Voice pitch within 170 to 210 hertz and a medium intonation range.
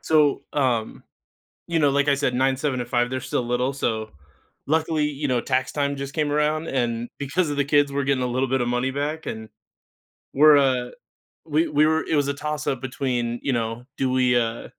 No: low, 135 Hz; average, 3.0 semitones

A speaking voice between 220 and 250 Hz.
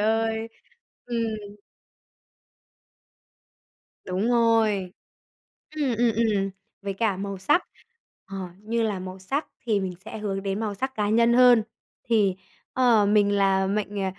No: high, 210 Hz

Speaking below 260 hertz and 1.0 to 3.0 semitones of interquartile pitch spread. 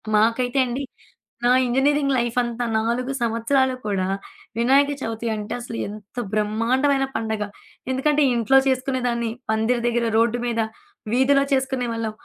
Yes: high, 240 Hz; narrow, 2.6 semitones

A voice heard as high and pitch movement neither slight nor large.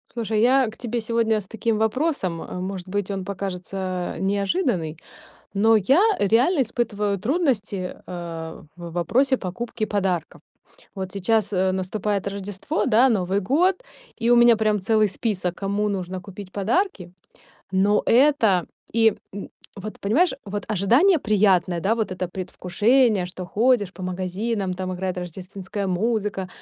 Yes: high, 200 Hz; average, 3.6 semitones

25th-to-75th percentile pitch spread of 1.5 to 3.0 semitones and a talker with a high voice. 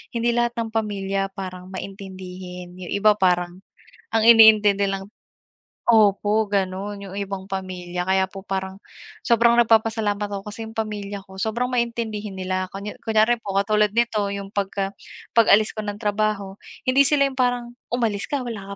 Yes: narrow, 2.6 semitones; high, 205 Hz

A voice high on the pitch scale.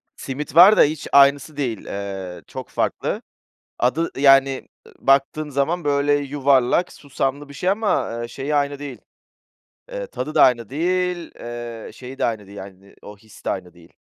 No: medium, 140 Hz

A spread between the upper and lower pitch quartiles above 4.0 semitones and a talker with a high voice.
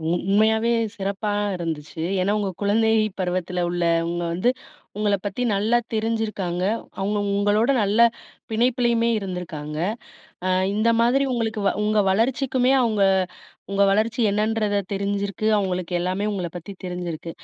No: average, 3.4 semitones; high, 200 Hz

